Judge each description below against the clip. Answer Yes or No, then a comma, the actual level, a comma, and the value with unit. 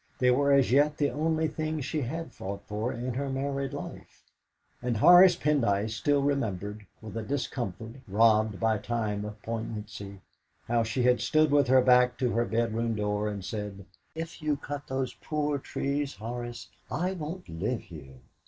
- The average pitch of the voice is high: No, low, 125 Hz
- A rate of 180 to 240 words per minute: No, average, 170 wpm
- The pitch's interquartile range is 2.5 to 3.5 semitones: No, average, 4.9 semitones